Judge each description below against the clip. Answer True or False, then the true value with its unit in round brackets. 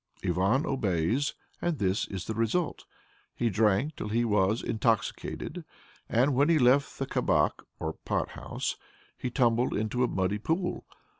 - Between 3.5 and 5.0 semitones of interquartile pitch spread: True (4.7 semitones)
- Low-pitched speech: True (115 Hz)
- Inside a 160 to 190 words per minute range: False (150 wpm)